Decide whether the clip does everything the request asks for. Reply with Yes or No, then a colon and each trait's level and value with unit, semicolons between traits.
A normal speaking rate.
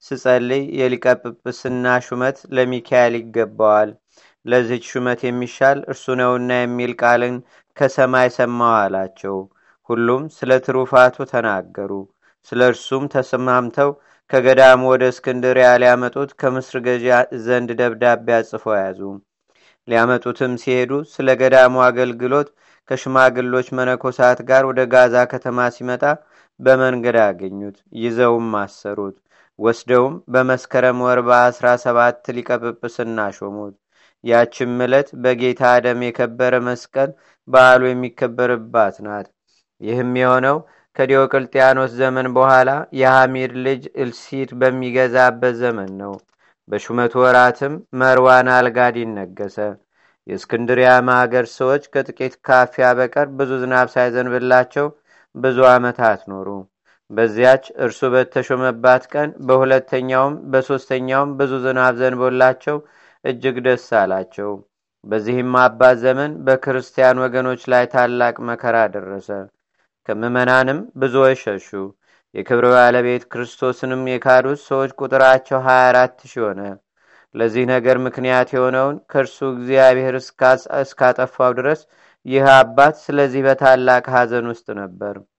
Yes: average, 100 wpm